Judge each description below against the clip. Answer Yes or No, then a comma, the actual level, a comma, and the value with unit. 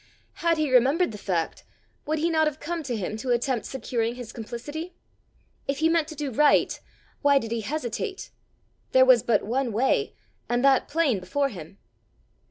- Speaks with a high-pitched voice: Yes, very high, 265 Hz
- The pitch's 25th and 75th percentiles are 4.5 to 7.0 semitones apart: Yes, average, 4.9 semitones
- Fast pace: No, average, 180 wpm